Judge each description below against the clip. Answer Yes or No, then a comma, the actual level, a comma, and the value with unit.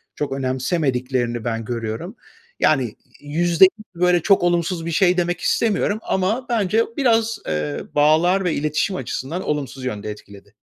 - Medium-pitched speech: Yes, medium, 160 Hz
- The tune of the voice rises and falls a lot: Yes, wide, 6.2 semitones